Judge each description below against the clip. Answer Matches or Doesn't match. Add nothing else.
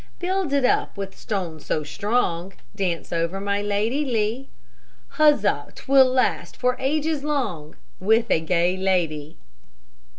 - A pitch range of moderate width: Doesn't match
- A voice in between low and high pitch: Doesn't match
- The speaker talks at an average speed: Doesn't match